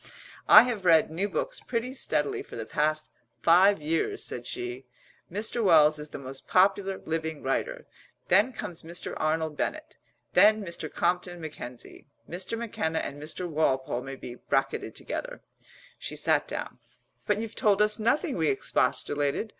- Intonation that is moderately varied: No, wide, 5.7 semitones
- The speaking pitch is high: No, medium, 170 Hz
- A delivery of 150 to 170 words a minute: Yes, average, 155 wpm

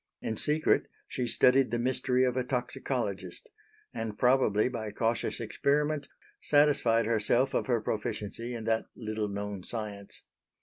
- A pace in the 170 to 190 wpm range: No, slow, 135 wpm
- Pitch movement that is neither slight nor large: Yes, average, 3.0 semitones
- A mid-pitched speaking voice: No, low, 120 Hz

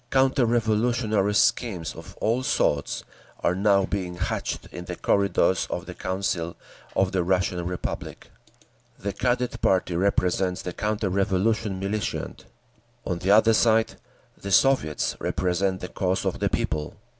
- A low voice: Yes, very low, 95 Hz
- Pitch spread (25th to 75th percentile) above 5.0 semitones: No, average, 3.2 semitones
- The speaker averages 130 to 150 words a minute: Yes, average, 140 wpm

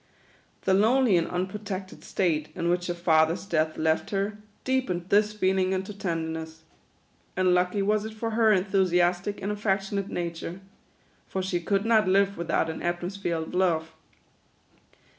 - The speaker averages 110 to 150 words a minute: Yes, average, 145 wpm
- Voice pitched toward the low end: No, medium, 185 Hz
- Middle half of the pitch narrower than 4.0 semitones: Yes, average, 2.8 semitones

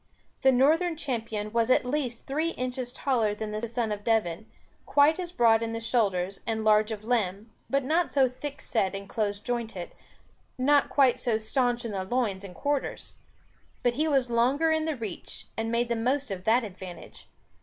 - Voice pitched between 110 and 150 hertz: No, high, 235 Hz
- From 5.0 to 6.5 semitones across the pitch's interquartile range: No, average, 3.9 semitones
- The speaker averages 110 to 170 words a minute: No, average, 185 wpm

